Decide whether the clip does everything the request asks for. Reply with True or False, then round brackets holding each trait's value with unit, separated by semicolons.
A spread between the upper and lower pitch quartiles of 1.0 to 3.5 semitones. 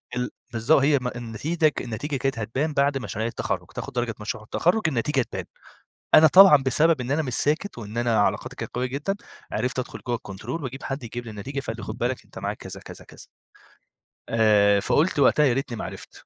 False (4.2 semitones)